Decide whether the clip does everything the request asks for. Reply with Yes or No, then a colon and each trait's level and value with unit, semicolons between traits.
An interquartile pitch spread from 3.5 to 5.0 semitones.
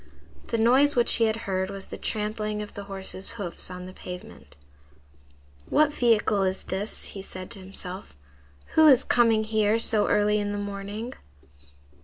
No: average, 2.8 semitones